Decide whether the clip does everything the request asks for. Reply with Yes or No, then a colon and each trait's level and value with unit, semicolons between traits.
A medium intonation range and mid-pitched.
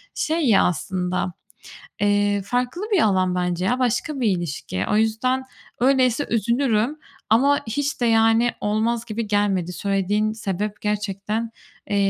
No: average, 3.5 semitones; high, 215 Hz